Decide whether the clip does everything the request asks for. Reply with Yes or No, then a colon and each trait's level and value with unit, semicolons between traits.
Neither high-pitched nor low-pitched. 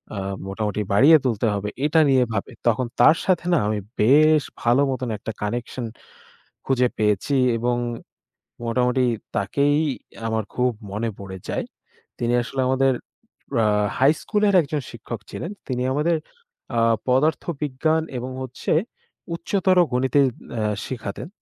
No: low, 130 Hz